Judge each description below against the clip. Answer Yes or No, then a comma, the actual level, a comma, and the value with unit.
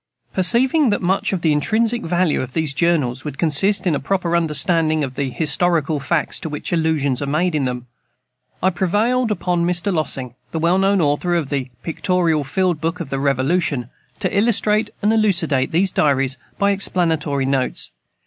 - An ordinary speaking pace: Yes, average, 175 wpm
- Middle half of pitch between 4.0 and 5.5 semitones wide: Yes, average, 4.7 semitones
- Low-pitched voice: No, medium, 165 Hz